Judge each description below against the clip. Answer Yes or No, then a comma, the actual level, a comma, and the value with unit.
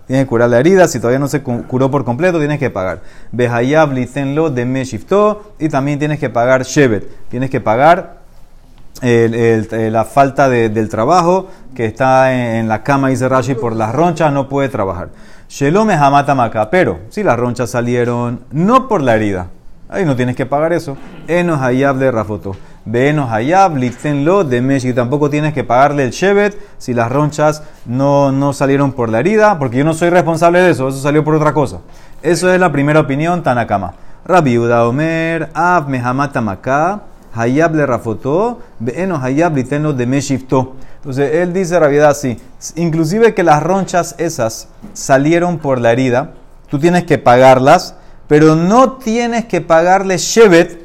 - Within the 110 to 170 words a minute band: Yes, average, 150 wpm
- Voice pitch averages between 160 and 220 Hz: No, medium, 140 Hz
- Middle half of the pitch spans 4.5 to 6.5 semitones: Yes, average, 5.2 semitones